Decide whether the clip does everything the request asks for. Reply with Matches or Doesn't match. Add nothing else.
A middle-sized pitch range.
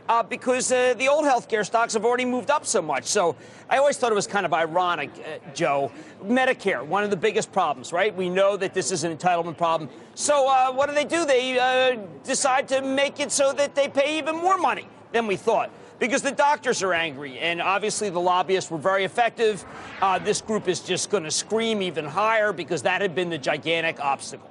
Doesn't match